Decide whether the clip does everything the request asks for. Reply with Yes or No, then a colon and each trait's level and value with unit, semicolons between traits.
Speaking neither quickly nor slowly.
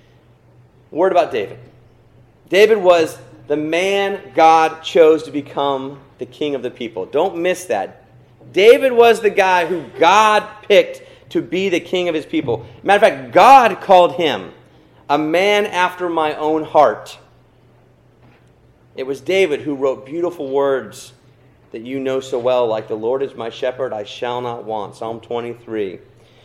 Yes: average, 155 wpm